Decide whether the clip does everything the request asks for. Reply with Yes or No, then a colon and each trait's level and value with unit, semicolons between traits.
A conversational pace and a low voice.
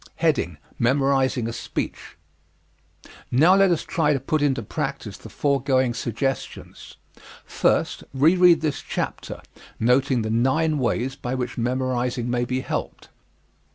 No: slow, 120 wpm; low, 130 Hz